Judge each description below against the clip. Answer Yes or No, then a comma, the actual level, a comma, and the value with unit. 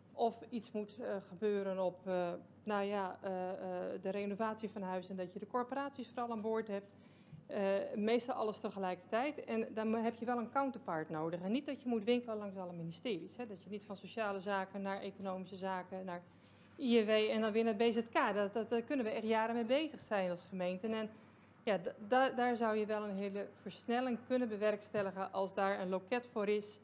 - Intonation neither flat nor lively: Yes, average, 3.3 semitones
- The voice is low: No, high, 210 Hz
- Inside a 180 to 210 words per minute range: Yes, average, 195 wpm